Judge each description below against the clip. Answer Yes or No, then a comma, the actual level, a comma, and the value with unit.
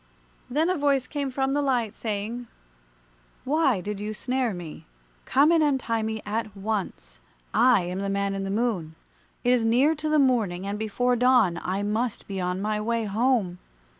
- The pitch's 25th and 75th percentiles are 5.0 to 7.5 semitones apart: No, average, 4.5 semitones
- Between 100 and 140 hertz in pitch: No, high, 225 Hz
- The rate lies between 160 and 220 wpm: Yes, average, 180 wpm